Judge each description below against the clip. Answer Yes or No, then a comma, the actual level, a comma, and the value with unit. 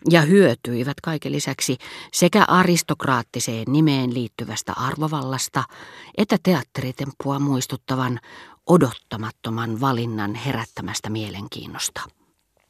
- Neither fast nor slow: No, slow, 75 wpm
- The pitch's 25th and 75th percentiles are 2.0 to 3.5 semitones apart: No, average, 4.9 semitones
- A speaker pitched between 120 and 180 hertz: Yes, low, 130 Hz